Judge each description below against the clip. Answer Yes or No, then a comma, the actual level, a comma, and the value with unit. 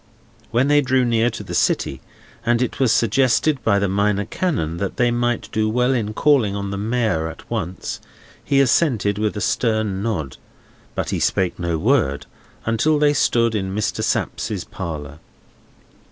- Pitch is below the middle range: Yes, low, 110 Hz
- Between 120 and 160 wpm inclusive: No, average, 170 wpm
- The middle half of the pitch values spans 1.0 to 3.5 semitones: No, average, 4.0 semitones